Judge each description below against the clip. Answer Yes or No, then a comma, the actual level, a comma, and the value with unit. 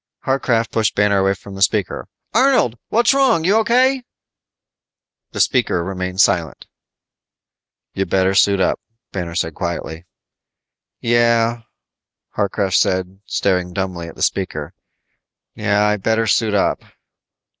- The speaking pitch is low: Yes, low, 100 Hz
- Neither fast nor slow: No, slow, 125 wpm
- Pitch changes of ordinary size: Yes, average, 4.0 semitones